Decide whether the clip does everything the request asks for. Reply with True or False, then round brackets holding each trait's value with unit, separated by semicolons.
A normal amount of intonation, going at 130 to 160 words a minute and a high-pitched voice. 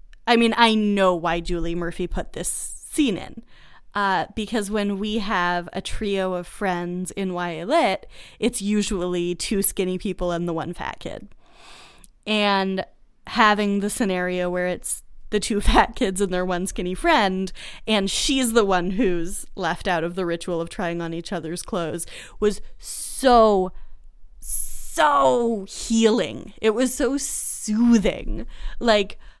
True (3.6 semitones; 145 wpm; 195 Hz)